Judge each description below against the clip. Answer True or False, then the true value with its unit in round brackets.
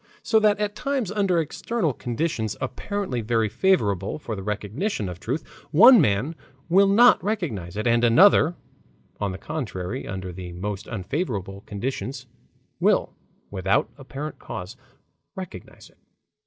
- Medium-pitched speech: False (125 Hz)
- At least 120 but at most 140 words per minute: True (135 wpm)